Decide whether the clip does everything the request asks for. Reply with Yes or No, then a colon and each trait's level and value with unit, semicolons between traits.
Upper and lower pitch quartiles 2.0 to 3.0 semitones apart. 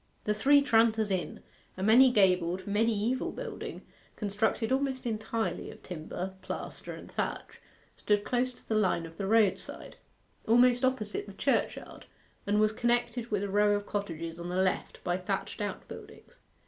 No: average, 3.9 semitones